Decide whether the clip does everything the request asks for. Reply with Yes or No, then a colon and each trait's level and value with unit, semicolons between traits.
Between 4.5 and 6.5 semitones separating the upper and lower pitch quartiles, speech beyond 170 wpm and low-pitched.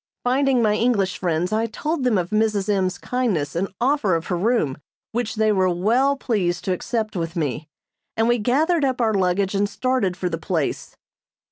No: average, 5.2 semitones; average, 190 wpm; high, 210 Hz